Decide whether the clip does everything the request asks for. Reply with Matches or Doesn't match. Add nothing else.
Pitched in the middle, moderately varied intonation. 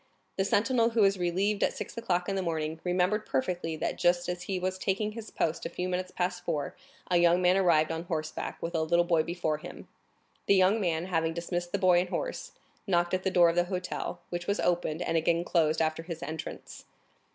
Doesn't match